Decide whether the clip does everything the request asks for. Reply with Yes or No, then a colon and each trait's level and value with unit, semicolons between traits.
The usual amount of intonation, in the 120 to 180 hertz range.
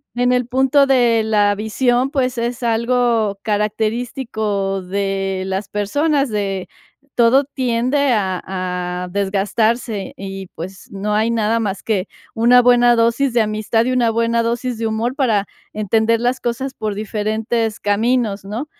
No: average, 3.2 semitones; high, 225 Hz